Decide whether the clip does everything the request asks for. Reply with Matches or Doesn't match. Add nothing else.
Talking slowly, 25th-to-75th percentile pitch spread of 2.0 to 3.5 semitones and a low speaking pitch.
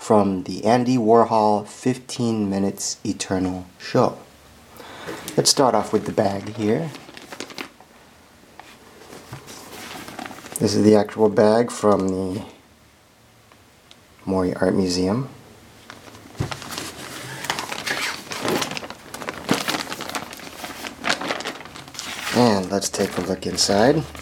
Matches